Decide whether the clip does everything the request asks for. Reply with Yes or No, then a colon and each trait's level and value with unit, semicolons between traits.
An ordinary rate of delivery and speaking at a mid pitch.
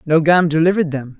Yes: average, 150 wpm; medium, 160 Hz